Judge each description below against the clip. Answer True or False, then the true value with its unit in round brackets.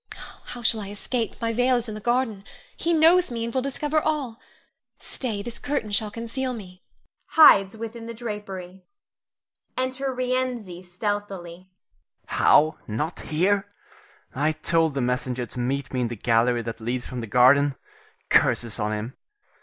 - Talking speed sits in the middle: True (160 wpm)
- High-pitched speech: True (205 Hz)